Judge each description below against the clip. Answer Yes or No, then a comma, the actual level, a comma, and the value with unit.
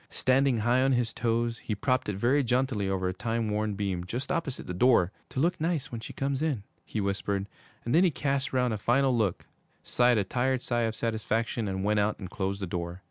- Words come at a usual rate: No, fast, 225 wpm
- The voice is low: Yes, low, 115 Hz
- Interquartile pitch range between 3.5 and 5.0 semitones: Yes, average, 4.3 semitones